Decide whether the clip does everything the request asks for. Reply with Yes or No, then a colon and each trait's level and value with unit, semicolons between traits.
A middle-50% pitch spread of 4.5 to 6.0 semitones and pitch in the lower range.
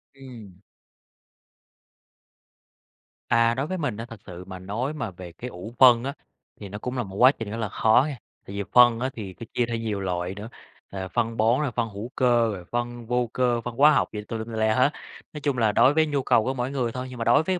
No: average, 3.4 semitones; low, 115 Hz